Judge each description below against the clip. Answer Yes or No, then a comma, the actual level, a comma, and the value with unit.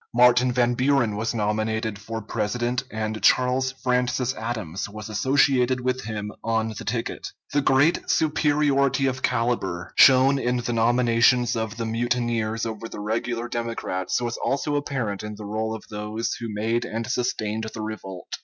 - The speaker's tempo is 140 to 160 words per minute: Yes, average, 155 wpm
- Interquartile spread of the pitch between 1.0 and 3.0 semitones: Yes, narrow, 2.6 semitones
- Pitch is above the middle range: No, low, 115 Hz